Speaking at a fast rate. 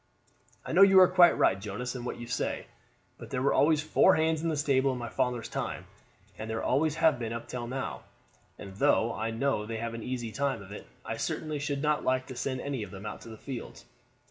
Yes: fast, 240 wpm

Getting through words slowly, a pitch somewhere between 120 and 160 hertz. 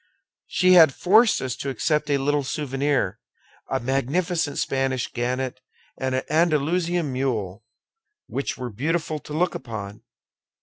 Yes: slow, 130 wpm; medium, 140 Hz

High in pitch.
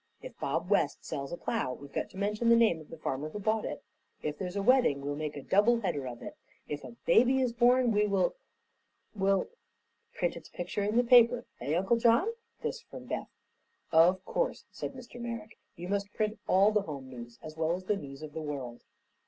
Yes: high, 195 Hz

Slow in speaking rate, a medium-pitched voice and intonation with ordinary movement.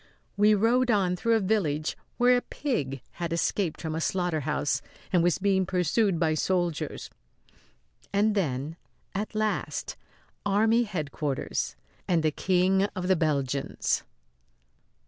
Yes: slow, 125 wpm; medium, 180 Hz; average, 4.9 semitones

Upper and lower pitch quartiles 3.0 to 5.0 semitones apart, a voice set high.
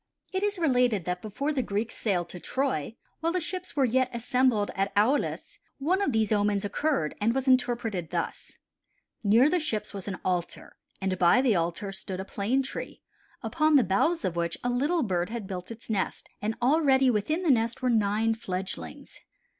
No: wide, 5.4 semitones; high, 225 Hz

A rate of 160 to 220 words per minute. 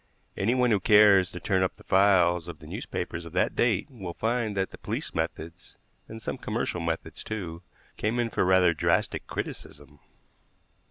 Yes: average, 170 wpm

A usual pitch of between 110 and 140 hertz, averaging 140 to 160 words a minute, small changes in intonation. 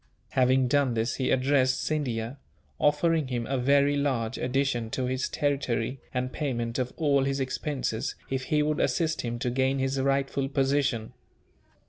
Yes: low, 135 Hz; average, 155 wpm; narrow, 2.0 semitones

